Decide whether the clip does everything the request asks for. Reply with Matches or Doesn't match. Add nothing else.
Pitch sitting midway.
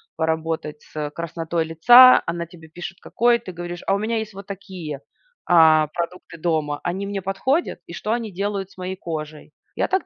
Matches